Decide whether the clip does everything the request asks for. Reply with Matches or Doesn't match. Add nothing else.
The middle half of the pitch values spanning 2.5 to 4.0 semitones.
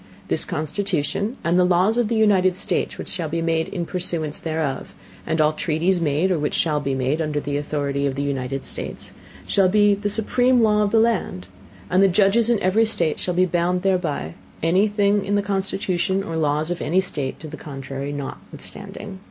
Doesn't match